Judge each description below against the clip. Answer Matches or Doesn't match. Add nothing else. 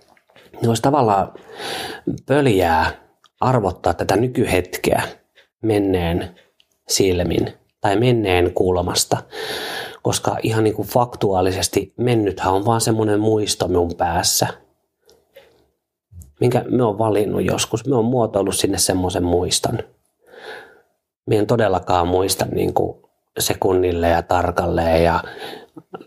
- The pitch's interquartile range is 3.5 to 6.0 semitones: Matches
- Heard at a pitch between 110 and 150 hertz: Doesn't match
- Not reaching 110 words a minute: Matches